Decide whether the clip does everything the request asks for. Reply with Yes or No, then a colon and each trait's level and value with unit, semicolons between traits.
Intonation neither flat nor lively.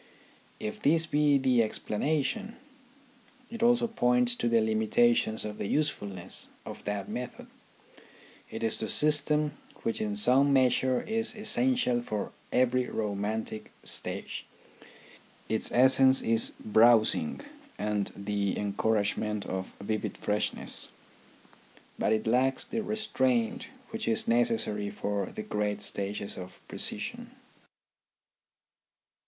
No: wide, 6.4 semitones